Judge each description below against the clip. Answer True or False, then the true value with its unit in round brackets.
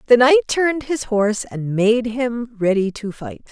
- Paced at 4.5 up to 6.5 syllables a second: False (4.3 syllables/s)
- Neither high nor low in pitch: False (230 Hz)